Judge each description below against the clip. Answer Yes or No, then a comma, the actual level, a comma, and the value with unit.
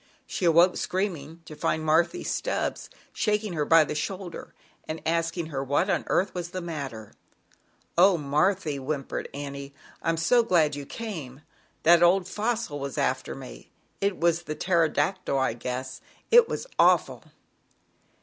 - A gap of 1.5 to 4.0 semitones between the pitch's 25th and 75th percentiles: No, average, 4.4 semitones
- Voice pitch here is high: No, medium, 165 Hz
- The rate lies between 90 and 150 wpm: Yes, average, 140 wpm